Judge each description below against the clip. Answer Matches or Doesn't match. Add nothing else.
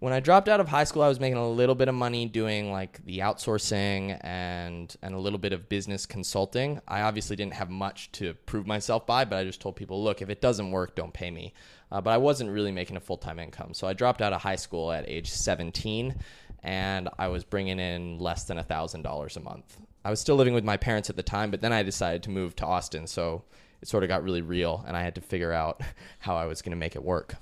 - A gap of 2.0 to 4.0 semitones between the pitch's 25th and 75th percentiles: Matches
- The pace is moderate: Doesn't match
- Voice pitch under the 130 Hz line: Matches